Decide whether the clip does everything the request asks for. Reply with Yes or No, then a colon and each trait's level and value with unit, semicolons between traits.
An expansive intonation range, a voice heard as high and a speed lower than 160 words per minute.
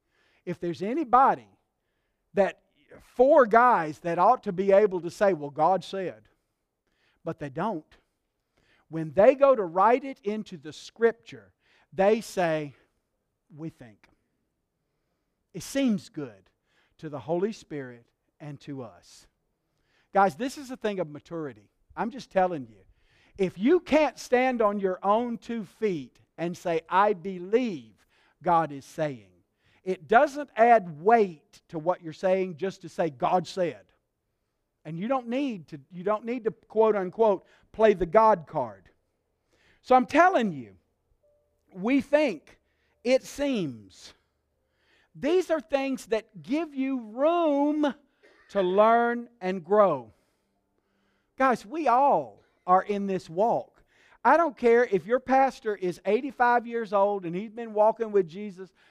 Yes: wide, 6.6 semitones; high, 195 Hz; average, 140 wpm